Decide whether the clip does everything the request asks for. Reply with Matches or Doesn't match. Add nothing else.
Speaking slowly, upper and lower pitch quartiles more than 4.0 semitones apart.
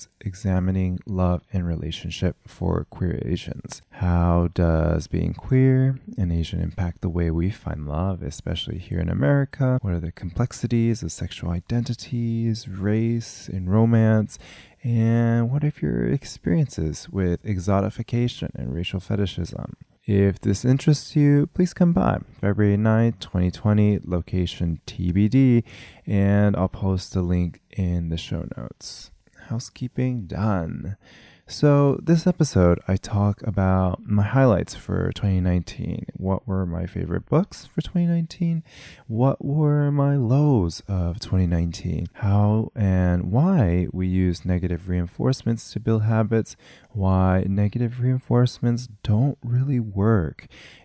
Matches